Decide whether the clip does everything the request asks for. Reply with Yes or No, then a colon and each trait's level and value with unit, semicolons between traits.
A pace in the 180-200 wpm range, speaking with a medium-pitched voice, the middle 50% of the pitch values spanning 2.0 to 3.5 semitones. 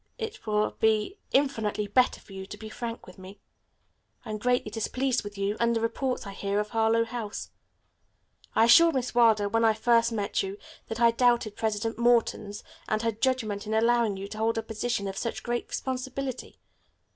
No: average, 190 wpm; high, 225 Hz; narrow, 2.4 semitones